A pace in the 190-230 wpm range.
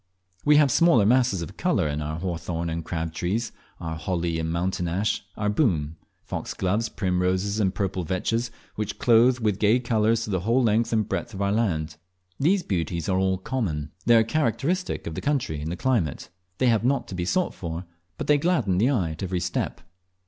Yes: average, 195 wpm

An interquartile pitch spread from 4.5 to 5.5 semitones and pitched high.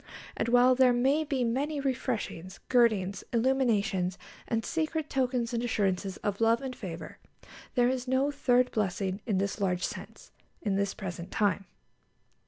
Yes: average, 4.8 semitones; high, 235 Hz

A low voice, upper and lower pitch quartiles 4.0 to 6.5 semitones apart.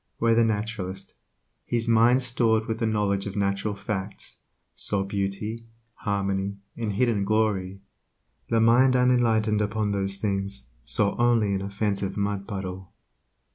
No: low, 105 Hz; narrow, 2.5 semitones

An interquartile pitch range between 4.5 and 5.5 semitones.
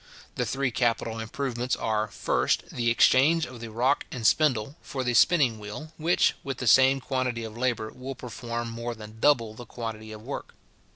No: average, 2.9 semitones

